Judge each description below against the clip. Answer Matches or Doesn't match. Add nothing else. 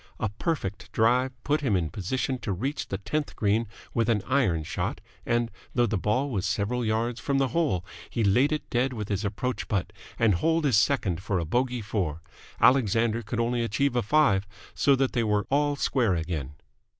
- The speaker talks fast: Doesn't match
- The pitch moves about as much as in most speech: Matches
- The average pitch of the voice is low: Matches